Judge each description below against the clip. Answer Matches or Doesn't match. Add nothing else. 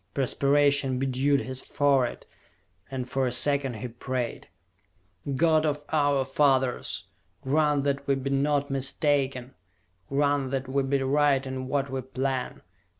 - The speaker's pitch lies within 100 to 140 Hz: Matches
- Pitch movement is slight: Matches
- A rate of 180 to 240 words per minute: Doesn't match